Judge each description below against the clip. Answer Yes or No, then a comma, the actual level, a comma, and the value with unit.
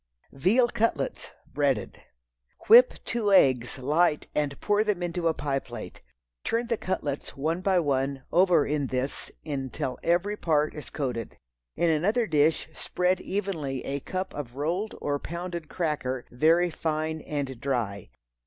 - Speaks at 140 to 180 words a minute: Yes, average, 145 wpm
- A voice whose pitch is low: No, medium, 155 Hz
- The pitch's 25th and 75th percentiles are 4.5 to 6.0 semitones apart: Yes, average, 4.8 semitones